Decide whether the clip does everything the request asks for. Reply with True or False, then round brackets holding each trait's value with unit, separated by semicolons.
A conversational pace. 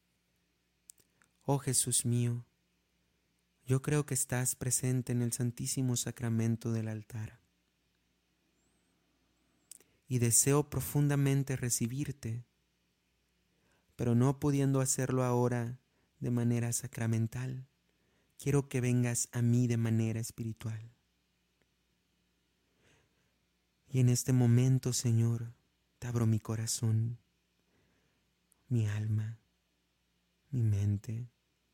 False (90 wpm)